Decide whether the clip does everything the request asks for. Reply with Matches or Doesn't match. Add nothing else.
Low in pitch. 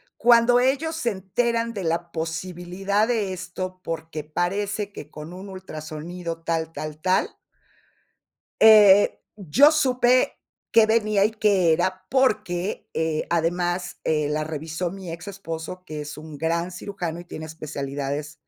Doesn't match